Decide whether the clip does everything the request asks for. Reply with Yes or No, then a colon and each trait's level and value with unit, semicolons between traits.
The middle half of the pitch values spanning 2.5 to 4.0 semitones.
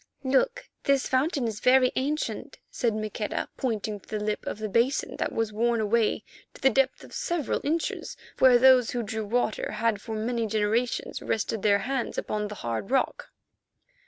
Yes: average, 3.5 semitones